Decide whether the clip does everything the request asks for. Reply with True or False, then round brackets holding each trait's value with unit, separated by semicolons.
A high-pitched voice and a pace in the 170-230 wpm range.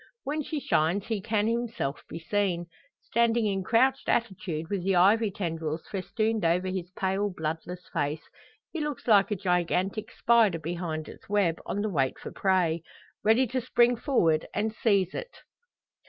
False (195 Hz; 160 wpm)